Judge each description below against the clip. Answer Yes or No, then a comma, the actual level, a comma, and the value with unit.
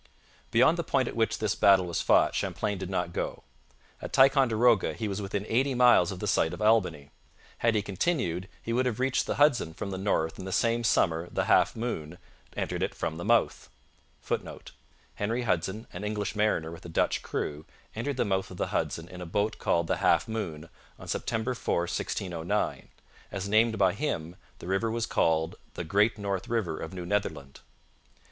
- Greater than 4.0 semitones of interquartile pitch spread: Yes, average, 4.7 semitones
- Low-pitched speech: Yes, low, 100 Hz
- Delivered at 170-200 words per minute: Yes, average, 180 wpm